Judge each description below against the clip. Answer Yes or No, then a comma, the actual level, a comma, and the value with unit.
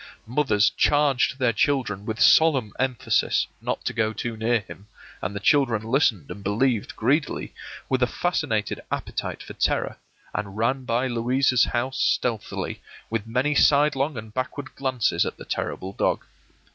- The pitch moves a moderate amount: Yes, average, 3.6 semitones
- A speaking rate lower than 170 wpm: Yes, average, 155 wpm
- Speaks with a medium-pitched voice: No, low, 120 Hz